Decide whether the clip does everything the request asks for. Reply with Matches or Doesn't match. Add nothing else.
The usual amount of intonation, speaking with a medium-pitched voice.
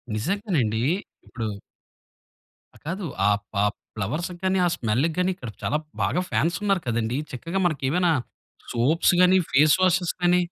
Doesn't match